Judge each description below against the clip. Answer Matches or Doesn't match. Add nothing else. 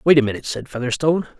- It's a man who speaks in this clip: Matches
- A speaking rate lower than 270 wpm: Matches